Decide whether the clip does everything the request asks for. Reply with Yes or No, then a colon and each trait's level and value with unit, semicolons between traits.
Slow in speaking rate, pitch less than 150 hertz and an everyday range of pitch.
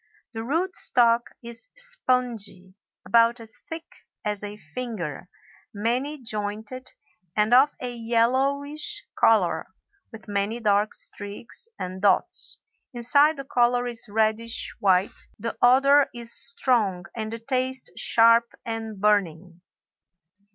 No: slow, 115 wpm; high, 230 Hz; average, 3.4 semitones